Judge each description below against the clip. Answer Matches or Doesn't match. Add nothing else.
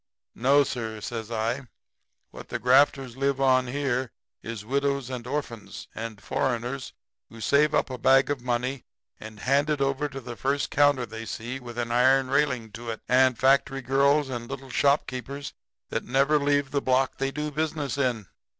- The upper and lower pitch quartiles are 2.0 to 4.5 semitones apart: Matches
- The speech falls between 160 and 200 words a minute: Matches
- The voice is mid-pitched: Doesn't match